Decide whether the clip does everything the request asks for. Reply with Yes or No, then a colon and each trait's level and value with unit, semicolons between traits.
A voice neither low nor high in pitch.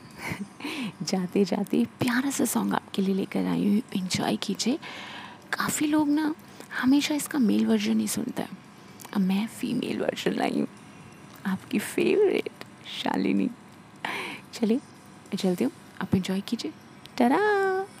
No: high, 225 Hz